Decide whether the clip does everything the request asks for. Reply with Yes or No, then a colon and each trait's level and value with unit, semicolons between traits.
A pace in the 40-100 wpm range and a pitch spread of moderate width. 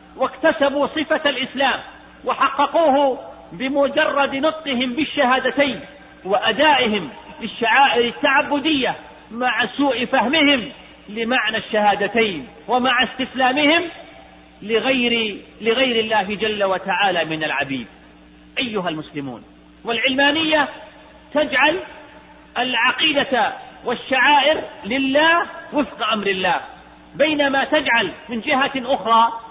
Yes: average, 80 wpm; average, 4.2 semitones